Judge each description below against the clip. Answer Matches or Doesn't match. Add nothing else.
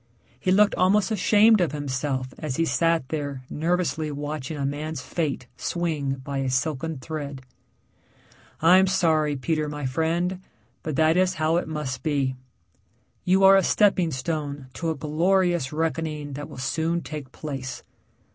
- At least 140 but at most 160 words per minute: Matches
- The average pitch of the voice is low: Doesn't match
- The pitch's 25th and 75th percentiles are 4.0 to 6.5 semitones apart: Doesn't match